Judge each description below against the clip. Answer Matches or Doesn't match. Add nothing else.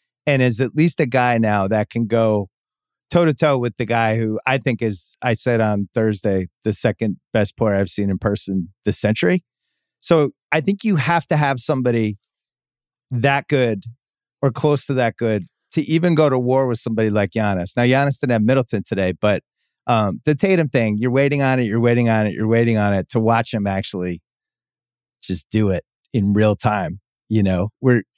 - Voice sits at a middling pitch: Doesn't match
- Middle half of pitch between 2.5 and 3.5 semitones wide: Doesn't match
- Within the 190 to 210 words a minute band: Matches